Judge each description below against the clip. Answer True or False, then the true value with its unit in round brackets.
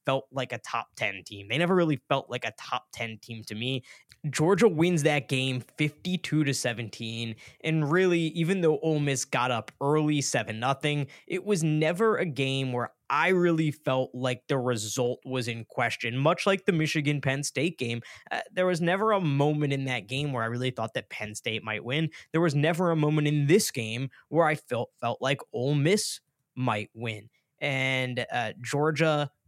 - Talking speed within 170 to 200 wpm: True (195 wpm)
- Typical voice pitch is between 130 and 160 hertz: True (140 Hz)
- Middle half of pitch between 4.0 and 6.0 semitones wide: True (4.3 semitones)